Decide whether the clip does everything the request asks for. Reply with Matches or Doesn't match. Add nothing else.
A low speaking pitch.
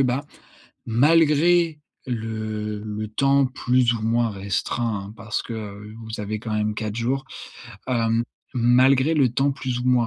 Matches